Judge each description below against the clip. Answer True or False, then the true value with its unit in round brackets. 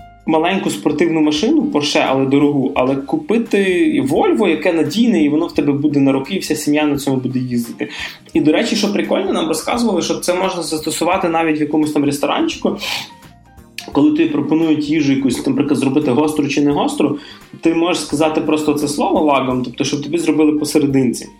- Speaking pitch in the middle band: True (155 Hz)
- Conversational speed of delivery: False (180 wpm)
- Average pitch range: True (4.2 semitones)